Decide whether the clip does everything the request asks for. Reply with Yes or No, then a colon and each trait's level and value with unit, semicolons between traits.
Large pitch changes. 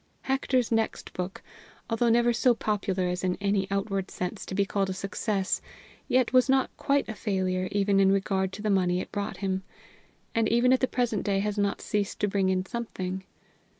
No: average, 3.1 semitones